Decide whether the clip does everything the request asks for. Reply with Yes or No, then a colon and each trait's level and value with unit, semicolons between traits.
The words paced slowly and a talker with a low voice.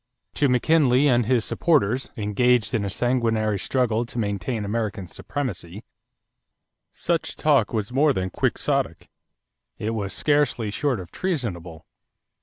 Yes: slow, 130 wpm; low, 115 Hz